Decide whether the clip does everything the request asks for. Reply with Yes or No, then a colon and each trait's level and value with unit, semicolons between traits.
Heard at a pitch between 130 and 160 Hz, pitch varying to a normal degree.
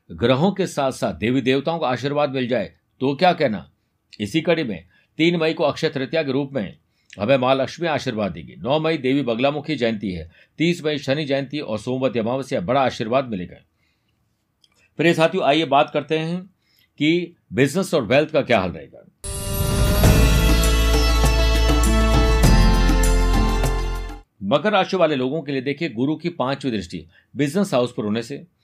No: low, 135 Hz; wide, 6.7 semitones